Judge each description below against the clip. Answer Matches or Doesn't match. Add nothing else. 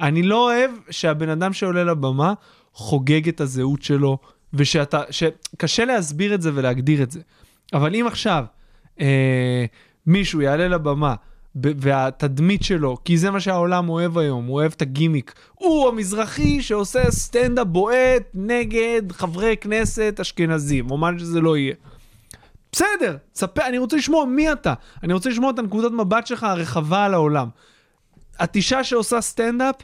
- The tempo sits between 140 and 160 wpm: Matches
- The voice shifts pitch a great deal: Matches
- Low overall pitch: Doesn't match